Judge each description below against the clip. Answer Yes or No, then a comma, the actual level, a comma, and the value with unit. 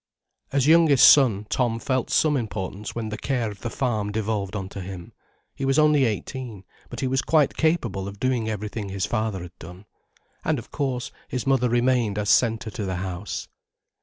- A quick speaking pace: No, average, 190 wpm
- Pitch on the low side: Yes, low, 115 Hz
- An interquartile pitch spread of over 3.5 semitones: Yes, average, 4.4 semitones